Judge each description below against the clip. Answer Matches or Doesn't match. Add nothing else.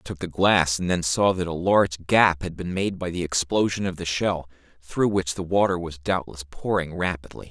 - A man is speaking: Matches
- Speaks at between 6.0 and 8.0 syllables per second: Doesn't match